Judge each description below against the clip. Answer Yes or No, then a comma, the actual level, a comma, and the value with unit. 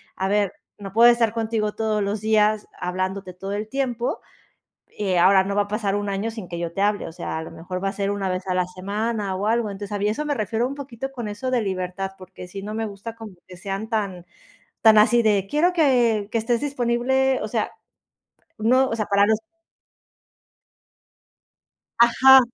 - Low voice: No, high, 210 Hz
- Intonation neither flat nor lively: Yes, average, 3.1 semitones